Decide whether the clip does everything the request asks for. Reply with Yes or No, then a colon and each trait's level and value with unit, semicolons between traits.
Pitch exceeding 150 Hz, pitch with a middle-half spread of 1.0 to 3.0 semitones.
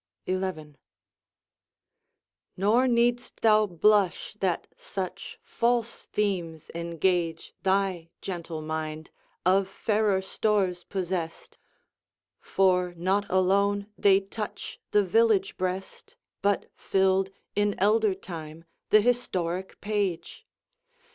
Yes: high, 190 Hz; average, 2.7 semitones